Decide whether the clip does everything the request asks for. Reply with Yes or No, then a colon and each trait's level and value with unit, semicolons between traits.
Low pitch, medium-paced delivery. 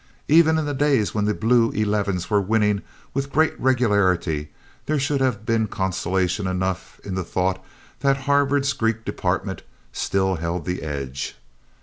Yes: low, 105 Hz; average, 150 wpm